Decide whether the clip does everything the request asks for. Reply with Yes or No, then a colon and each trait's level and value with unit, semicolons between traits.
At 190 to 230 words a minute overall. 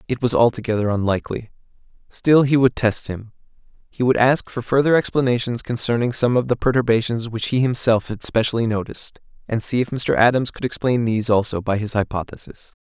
No: average, 180 wpm